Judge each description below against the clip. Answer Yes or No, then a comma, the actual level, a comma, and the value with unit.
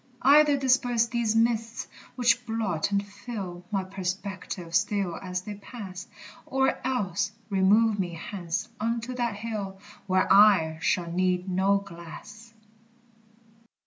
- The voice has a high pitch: Yes, high, 200 Hz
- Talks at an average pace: No, slow, 120 wpm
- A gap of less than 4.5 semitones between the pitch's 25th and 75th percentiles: Yes, average, 3.7 semitones